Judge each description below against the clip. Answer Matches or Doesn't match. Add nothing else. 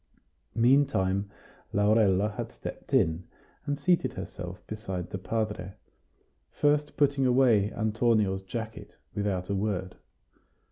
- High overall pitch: Doesn't match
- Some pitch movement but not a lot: Matches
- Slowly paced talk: Matches